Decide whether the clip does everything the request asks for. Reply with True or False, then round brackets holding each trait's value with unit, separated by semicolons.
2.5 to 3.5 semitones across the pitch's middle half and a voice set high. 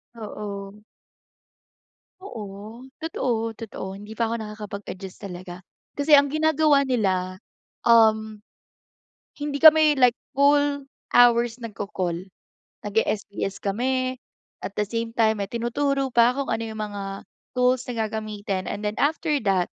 False (4.2 semitones; 225 Hz)